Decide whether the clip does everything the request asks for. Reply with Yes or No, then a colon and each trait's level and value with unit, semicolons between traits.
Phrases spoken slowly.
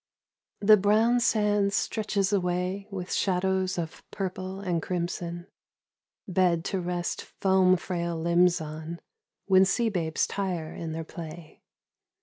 Yes: slow, 125 wpm